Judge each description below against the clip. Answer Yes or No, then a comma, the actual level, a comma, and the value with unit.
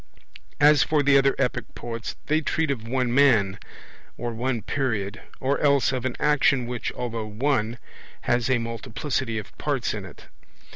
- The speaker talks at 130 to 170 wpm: Yes, average, 160 wpm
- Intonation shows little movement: No, average, 3.2 semitones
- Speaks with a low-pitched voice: Yes, low, 125 Hz